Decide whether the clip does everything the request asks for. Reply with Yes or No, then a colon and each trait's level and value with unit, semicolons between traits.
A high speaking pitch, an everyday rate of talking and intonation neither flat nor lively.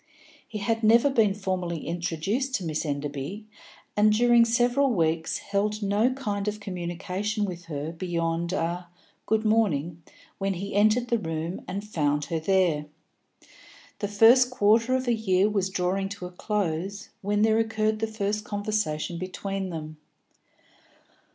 Yes: high, 200 Hz; average, 145 wpm; average, 4.0 semitones